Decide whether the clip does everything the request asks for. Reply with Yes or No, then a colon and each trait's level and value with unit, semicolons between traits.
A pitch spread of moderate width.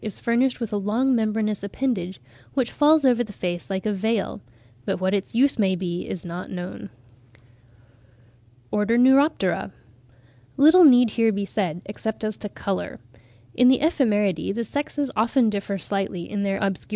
Yes: average, 4.3 semitones